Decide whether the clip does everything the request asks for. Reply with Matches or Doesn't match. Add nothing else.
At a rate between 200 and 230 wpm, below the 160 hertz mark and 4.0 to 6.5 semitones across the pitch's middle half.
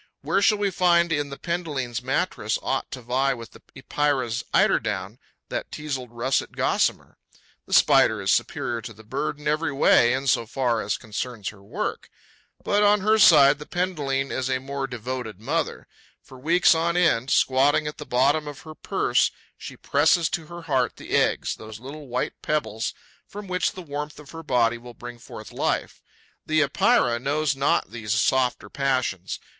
Doesn't match